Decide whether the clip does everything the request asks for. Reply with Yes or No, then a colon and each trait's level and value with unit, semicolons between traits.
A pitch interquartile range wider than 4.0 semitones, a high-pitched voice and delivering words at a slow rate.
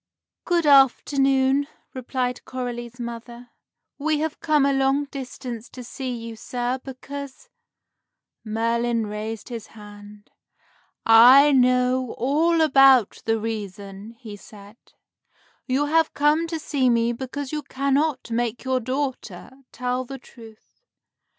No: average, 3.2 semitones; very high, 255 Hz; slow, 125 wpm